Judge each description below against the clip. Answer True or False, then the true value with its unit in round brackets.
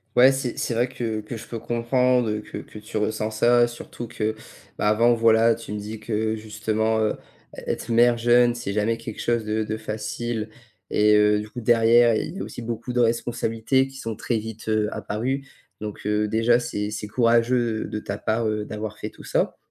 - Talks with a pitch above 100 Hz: True (110 Hz)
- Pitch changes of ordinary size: False (1.8 semitones)